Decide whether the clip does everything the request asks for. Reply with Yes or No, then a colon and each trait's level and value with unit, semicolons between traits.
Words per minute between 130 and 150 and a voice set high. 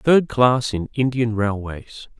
No: slow, 135 wpm; low, 120 Hz